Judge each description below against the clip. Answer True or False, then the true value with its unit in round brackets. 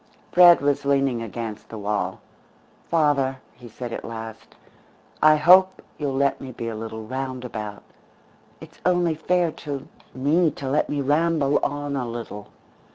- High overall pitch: False (135 Hz)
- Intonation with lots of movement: False (4.8 semitones)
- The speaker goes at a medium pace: True (150 wpm)